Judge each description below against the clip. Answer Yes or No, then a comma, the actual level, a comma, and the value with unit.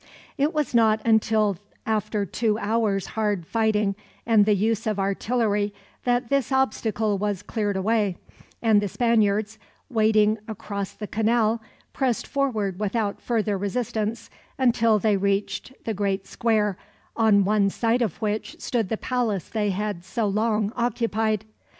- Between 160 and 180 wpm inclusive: No, average, 140 wpm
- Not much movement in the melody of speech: Yes, narrow, 2.0 semitones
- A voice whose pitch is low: No, high, 215 Hz